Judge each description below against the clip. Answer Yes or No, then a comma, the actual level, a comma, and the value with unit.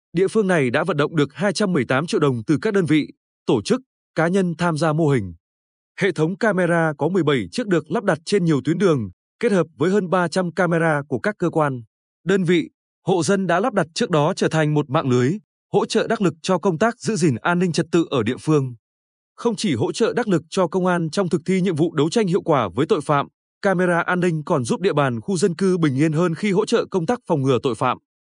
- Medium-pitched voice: Yes, medium, 175 Hz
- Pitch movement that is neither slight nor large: Yes, average, 4.4 semitones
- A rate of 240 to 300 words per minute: Yes, fast, 250 wpm